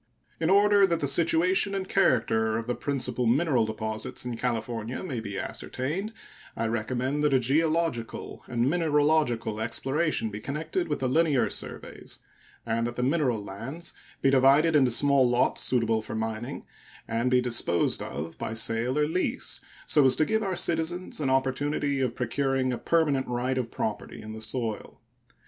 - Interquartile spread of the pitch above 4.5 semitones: Yes, average, 5.1 semitones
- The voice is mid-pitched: No, low, 130 Hz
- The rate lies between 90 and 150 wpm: No, average, 165 wpm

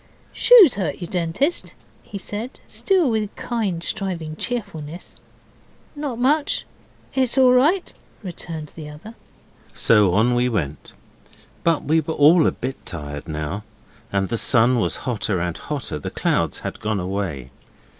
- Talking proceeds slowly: No, average, 145 wpm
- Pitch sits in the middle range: Yes, medium, 155 Hz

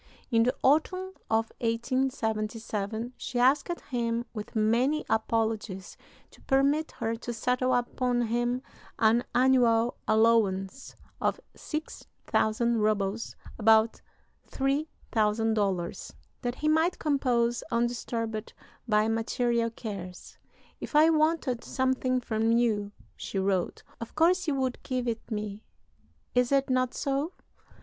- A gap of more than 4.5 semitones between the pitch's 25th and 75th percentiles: No, average, 2.9 semitones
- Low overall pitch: No, high, 235 Hz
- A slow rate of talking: Yes, slow, 115 wpm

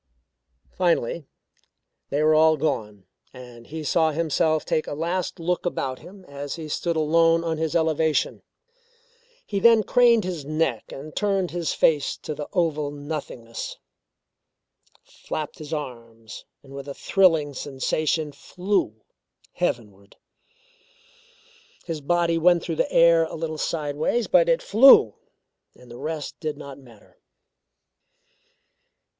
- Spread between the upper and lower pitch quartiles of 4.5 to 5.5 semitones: No, average, 3.1 semitones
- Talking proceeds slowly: Yes, slow, 130 wpm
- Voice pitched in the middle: Yes, medium, 155 Hz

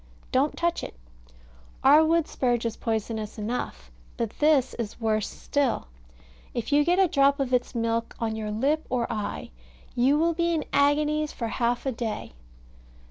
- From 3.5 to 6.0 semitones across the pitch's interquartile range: Yes, average, 4.7 semitones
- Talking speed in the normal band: Yes, average, 165 wpm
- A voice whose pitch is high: Yes, very high, 250 Hz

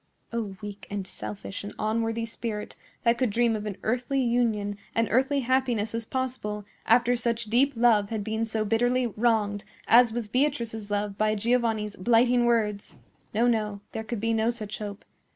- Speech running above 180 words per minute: No, average, 170 wpm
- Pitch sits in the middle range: No, high, 225 Hz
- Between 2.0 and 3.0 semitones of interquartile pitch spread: Yes, narrow, 2.4 semitones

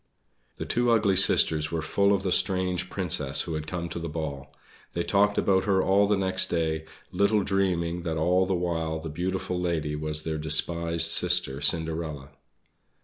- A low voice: Yes, very low, 85 Hz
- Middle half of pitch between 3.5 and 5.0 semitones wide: No, average, 3.0 semitones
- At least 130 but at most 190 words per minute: Yes, average, 175 wpm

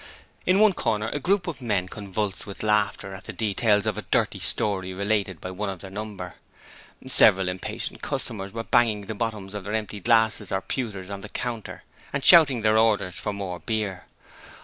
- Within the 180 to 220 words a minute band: Yes, average, 190 wpm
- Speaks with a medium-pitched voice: No, low, 105 Hz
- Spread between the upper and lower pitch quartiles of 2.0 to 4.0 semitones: Yes, narrow, 2.6 semitones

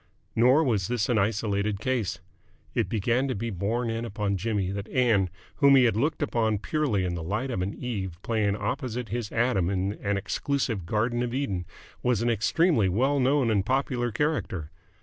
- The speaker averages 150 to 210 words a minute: Yes, average, 185 wpm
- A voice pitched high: No, low, 115 Hz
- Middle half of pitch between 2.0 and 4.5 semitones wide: Yes, average, 4.1 semitones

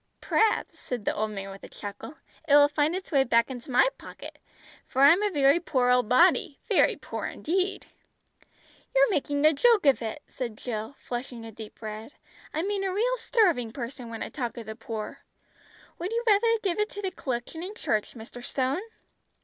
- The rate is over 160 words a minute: Yes, average, 195 wpm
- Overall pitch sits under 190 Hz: No, very high, 275 Hz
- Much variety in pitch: Yes, wide, 8.0 semitones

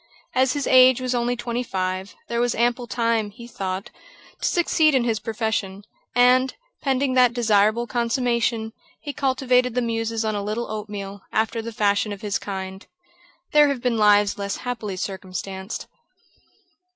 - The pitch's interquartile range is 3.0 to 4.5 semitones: Yes, average, 3.3 semitones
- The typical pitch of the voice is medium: No, high, 230 Hz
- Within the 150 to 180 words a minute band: Yes, average, 155 wpm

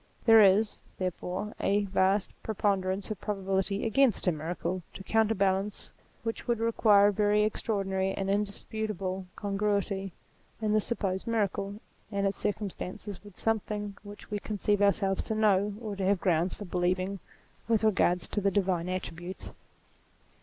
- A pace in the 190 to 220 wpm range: No, average, 145 wpm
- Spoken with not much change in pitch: Yes, narrow, 1.8 semitones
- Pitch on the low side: No, high, 200 Hz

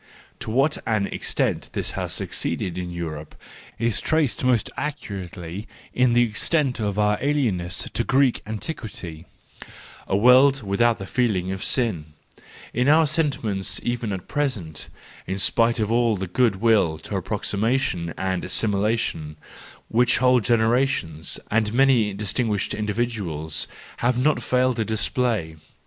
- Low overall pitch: Yes, low, 110 Hz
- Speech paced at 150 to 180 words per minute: No, slow, 135 wpm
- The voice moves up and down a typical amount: Yes, average, 4.7 semitones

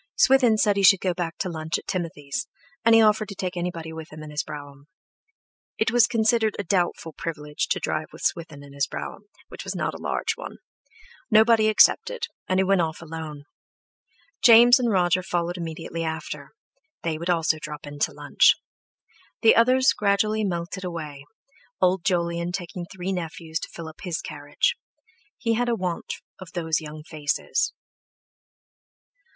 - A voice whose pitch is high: No, medium, 175 Hz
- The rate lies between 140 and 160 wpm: No, average, 170 wpm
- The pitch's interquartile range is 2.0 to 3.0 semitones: No, average, 4.7 semitones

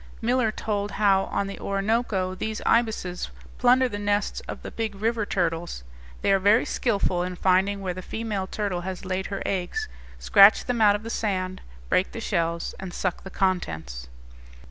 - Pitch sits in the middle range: No, high, 195 Hz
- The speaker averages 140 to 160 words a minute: No, average, 175 wpm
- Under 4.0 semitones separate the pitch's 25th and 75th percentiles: Yes, average, 2.9 semitones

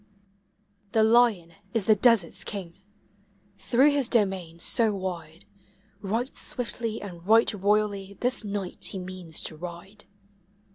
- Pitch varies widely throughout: No, average, 3.7 semitones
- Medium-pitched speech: No, high, 200 Hz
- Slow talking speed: Yes, slow, 125 wpm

